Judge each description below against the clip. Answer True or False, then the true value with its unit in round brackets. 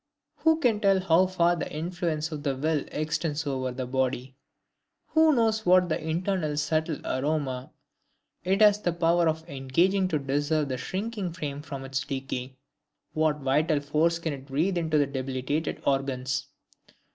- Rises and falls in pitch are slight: False (4.4 semitones)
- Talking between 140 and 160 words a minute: True (150 wpm)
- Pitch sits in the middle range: True (155 Hz)